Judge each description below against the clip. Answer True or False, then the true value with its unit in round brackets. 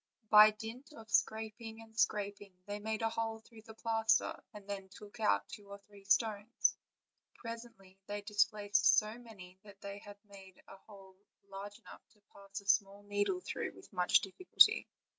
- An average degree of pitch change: False (1.9 semitones)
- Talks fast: False (180 wpm)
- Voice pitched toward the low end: False (205 Hz)